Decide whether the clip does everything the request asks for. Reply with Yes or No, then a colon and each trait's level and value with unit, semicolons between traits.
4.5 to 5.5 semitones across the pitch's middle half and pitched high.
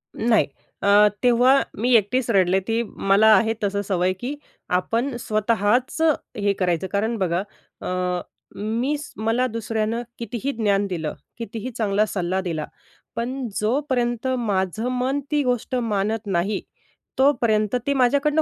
No: average, 3.8 semitones; high, 225 Hz